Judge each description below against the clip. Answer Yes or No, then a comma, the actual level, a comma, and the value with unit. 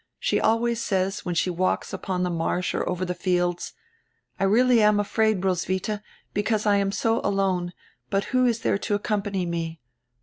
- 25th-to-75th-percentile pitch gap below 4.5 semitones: Yes, average, 2.9 semitones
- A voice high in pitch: Yes, high, 195 Hz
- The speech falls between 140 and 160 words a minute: No, average, 175 wpm